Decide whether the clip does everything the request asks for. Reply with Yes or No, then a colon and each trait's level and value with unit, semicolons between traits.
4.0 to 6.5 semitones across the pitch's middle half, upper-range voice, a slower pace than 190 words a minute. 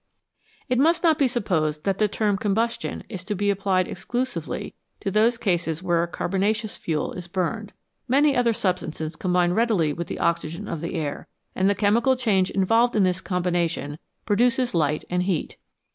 Yes: average, 4.7 semitones; high, 195 Hz; average, 175 wpm